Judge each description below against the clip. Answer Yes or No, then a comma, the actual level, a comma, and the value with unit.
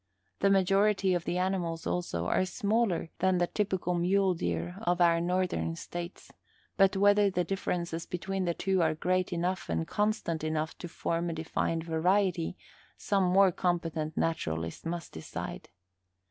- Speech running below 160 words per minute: Yes, average, 150 wpm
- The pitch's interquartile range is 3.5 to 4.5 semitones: No, narrow, 2.6 semitones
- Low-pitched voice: No, medium, 175 Hz